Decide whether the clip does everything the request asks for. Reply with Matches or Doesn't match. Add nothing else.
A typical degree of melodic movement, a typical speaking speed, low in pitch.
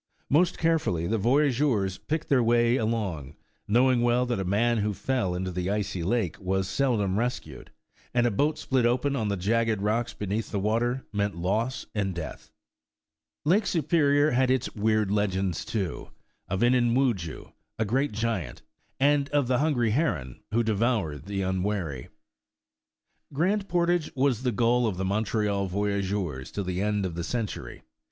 Matches